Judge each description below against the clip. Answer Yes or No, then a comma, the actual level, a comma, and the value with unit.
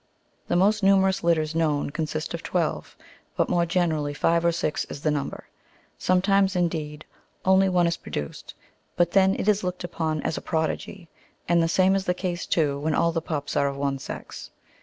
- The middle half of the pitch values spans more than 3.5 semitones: No, average, 3.0 semitones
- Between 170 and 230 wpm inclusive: Yes, average, 195 wpm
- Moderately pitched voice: Yes, medium, 170 Hz